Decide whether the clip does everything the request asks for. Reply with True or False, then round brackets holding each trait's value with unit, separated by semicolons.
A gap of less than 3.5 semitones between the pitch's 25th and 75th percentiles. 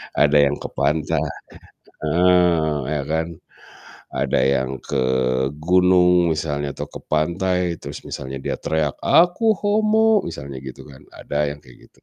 False (4.0 semitones)